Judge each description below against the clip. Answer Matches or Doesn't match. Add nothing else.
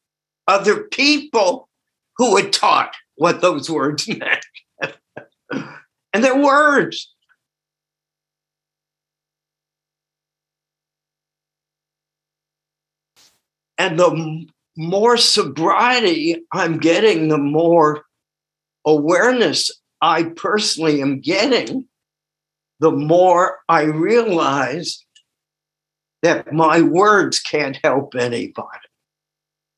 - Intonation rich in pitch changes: Doesn't match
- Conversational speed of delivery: Doesn't match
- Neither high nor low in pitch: Matches